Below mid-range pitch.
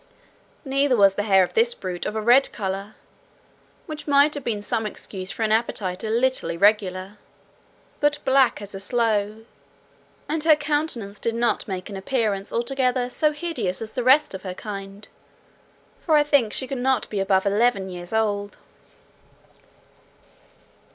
No: high, 220 Hz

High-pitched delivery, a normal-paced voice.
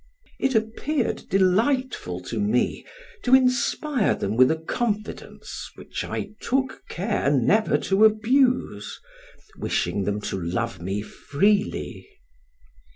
No: high, 205 Hz; slow, 110 wpm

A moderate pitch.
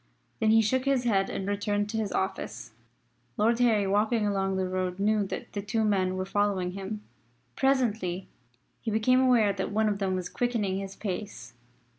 No: high, 205 Hz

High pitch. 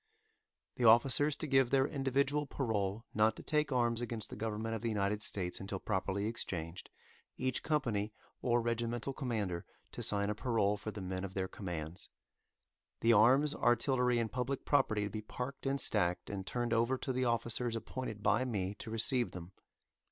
No: low, 115 Hz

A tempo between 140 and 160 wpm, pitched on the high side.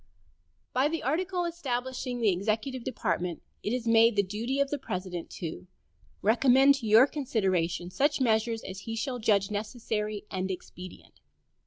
Yes: average, 150 wpm; high, 225 Hz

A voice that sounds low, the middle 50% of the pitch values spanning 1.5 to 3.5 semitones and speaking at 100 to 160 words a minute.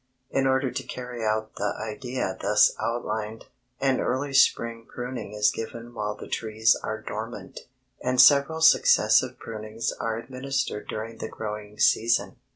Yes: low, 115 Hz; average, 3.0 semitones; average, 145 wpm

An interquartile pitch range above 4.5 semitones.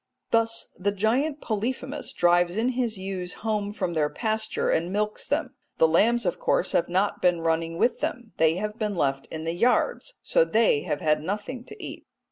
Yes: average, 5.0 semitones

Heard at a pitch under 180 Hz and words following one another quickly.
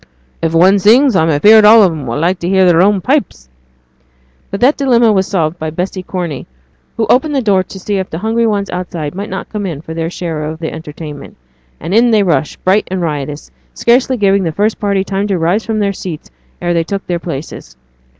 No: medium, 185 Hz; fast, 220 wpm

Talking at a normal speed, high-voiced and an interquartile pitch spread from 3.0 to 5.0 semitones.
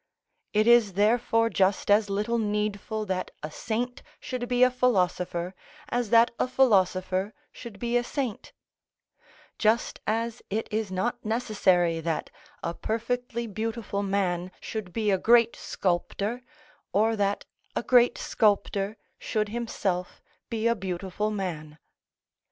No: slow, 130 wpm; high, 215 Hz; average, 3.4 semitones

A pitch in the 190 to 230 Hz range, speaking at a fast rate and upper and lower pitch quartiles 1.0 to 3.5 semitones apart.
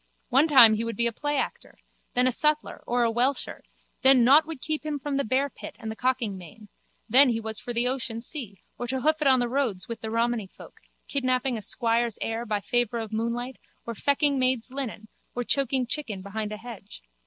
No: high, 245 Hz; fast, 210 wpm; average, 3.1 semitones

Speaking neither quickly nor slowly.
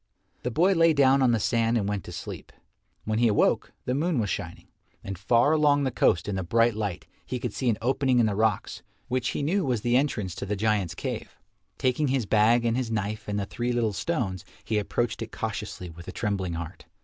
No: fast, 225 wpm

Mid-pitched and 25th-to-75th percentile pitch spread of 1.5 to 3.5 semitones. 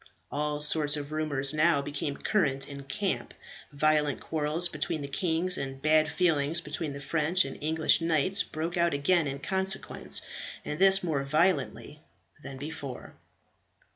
Yes: medium, 150 Hz; average, 2.7 semitones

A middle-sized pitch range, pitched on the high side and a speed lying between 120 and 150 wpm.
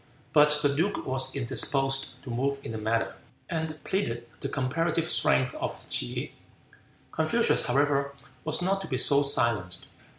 No: average, 3.6 semitones; medium, 140 Hz; average, 145 wpm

